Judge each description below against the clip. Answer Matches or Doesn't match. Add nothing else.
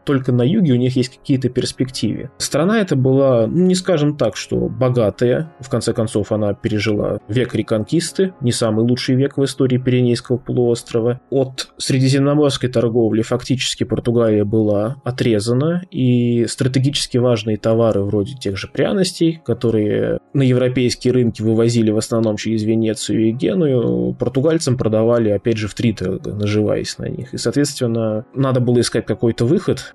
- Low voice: Matches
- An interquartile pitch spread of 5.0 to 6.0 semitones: Doesn't match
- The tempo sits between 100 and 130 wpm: Doesn't match